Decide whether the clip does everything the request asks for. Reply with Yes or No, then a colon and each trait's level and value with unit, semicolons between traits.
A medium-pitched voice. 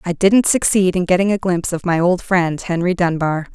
Yes: medium, 180 Hz